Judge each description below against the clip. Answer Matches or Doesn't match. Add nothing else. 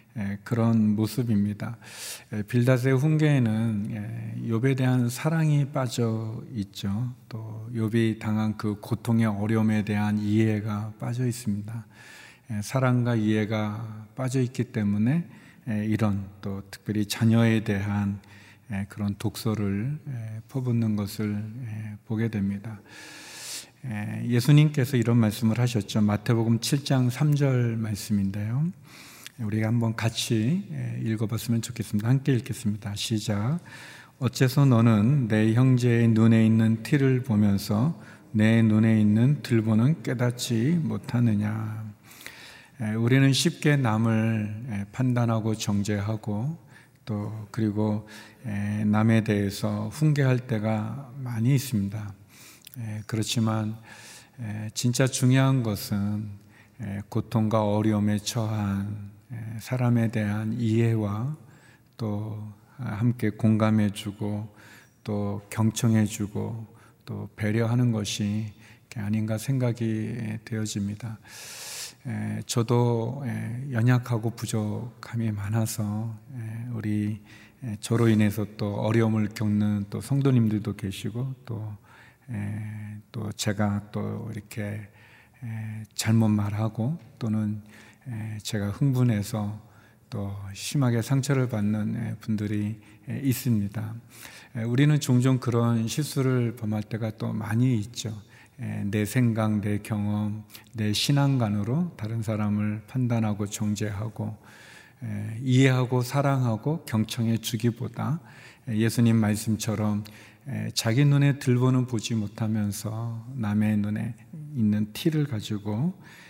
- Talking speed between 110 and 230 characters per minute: Matches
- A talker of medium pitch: Doesn't match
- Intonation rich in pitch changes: Doesn't match